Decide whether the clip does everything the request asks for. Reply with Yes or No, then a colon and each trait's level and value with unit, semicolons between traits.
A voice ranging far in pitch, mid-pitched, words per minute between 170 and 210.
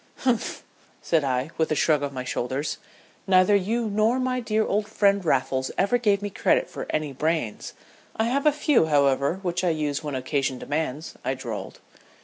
Yes: wide, 7.4 semitones; medium, 160 Hz; average, 180 wpm